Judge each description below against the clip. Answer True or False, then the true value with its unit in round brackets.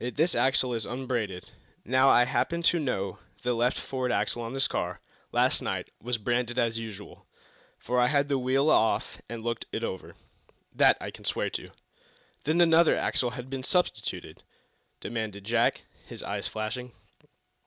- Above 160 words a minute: True (170 wpm)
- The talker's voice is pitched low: True (125 Hz)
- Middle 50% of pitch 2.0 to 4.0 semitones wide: True (2.8 semitones)